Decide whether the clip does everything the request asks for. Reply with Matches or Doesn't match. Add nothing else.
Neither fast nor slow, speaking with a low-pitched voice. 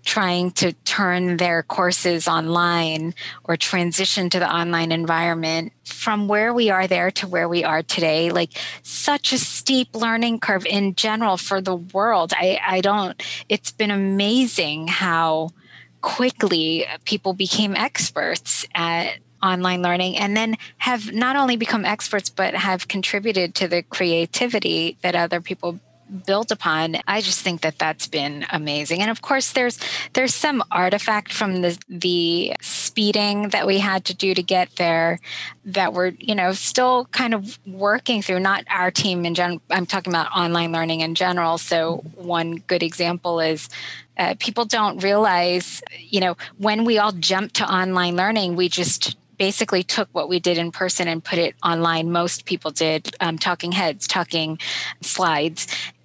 Doesn't match